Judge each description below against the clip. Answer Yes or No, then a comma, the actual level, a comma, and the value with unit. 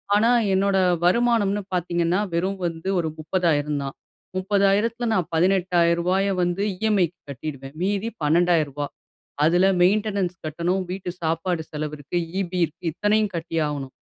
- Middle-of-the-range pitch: Yes, medium, 180 Hz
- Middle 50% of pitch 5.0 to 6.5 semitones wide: No, average, 3.3 semitones